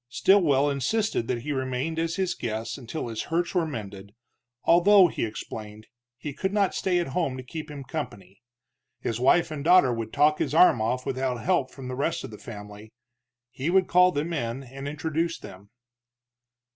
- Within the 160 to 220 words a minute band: Yes, average, 185 wpm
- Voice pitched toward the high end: No, medium, 140 Hz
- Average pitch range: No, wide, 6.1 semitones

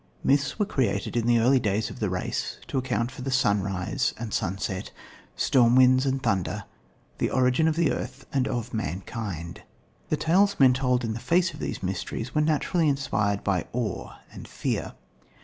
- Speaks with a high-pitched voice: No, low, 125 Hz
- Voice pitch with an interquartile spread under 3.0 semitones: No, average, 4.8 semitones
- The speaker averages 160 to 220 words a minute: Yes, average, 175 wpm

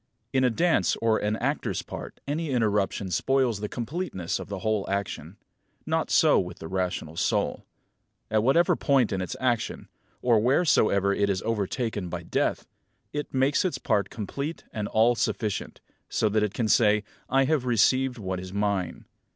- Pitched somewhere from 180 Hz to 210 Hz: No, low, 110 Hz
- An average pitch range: Yes, average, 4.7 semitones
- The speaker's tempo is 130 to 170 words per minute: Yes, average, 165 wpm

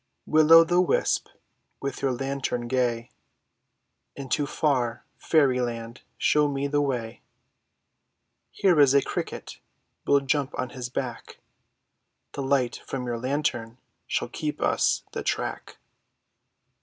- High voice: No, low, 135 Hz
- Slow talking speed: Yes, slow, 130 wpm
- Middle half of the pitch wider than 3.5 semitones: No, average, 2.8 semitones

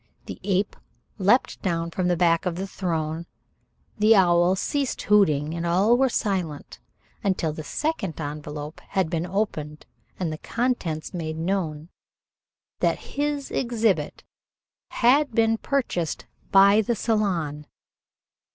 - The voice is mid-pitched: Yes, medium, 180 Hz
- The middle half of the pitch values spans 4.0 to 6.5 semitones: Yes, average, 5.2 semitones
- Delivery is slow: Yes, slow, 125 wpm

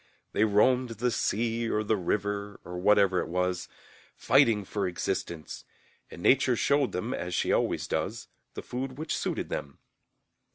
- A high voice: No, low, 105 Hz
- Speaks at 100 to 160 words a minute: Yes, average, 155 wpm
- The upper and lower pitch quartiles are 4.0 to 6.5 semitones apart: Yes, average, 4.7 semitones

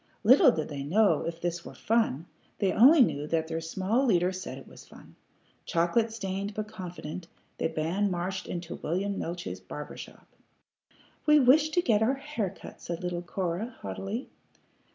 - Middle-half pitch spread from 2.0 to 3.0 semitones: No, average, 4.9 semitones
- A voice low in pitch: No, high, 190 Hz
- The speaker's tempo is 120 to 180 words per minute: Yes, average, 170 wpm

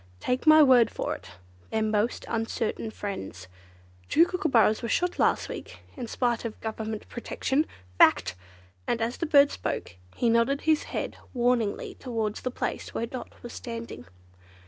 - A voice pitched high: Yes, high, 235 Hz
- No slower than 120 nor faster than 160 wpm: Yes, average, 155 wpm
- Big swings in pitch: No, average, 3.2 semitones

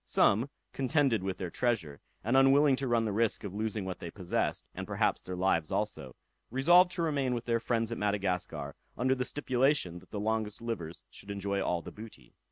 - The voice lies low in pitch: Yes, low, 110 Hz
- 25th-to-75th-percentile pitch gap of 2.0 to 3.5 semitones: No, average, 5.3 semitones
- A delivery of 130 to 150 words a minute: No, average, 195 wpm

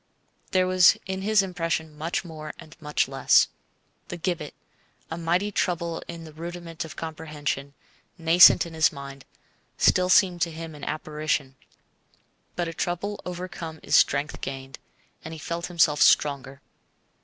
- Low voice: No, medium, 165 Hz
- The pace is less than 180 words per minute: Yes, average, 145 wpm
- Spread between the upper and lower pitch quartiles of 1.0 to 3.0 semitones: Yes, narrow, 2.5 semitones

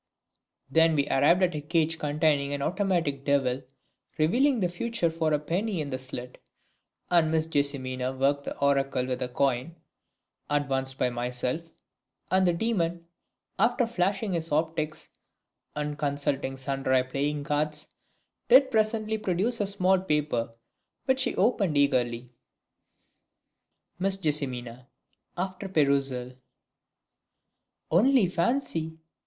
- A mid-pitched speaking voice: Yes, medium, 155 Hz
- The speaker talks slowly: Yes, slow, 120 wpm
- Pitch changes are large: No, average, 5.0 semitones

